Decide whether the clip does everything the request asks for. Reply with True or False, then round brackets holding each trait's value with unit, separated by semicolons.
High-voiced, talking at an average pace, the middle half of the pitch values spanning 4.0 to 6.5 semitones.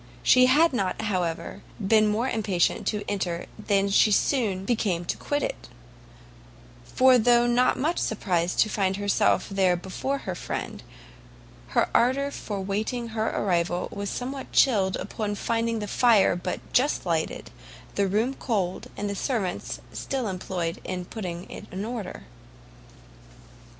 True (205 Hz; 145 wpm; 4.4 semitones)